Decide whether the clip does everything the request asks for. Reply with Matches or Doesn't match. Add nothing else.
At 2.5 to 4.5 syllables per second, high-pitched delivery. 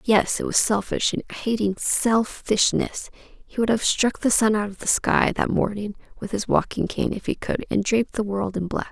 Doesn't match